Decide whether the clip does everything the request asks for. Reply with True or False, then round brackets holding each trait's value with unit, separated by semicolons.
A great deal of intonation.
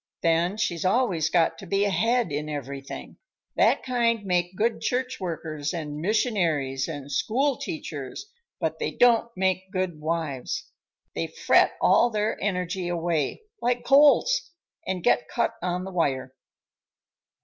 True (6.1 semitones)